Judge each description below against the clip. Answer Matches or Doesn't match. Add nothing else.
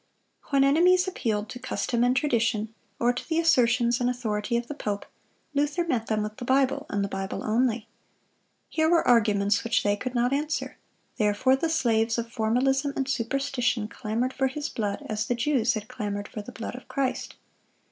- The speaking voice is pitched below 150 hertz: Doesn't match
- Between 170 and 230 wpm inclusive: Matches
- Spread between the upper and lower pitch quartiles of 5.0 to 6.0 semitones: Doesn't match